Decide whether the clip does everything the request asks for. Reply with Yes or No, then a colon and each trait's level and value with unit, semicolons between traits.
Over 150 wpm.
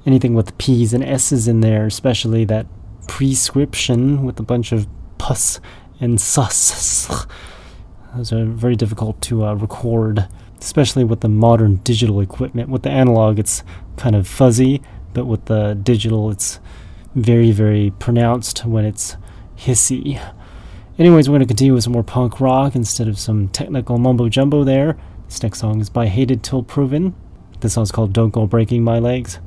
Yes: average, 165 wpm